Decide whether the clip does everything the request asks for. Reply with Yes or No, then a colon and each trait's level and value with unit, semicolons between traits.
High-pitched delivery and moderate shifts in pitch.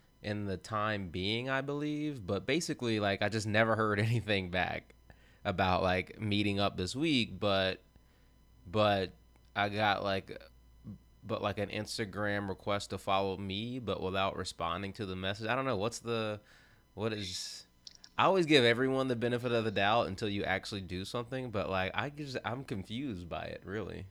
No: low, 100 Hz; average, 3.2 semitones